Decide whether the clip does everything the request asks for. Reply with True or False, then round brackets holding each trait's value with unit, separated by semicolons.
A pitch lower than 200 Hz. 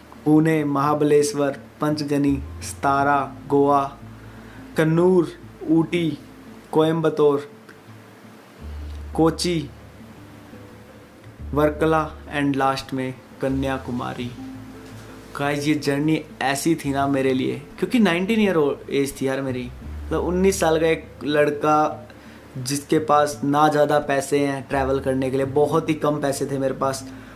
True (140 Hz)